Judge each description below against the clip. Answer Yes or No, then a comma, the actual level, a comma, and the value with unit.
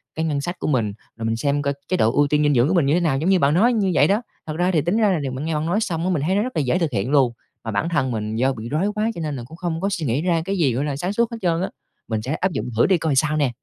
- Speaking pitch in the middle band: Yes, medium, 155 Hz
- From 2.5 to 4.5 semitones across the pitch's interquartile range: No, average, 5.0 semitones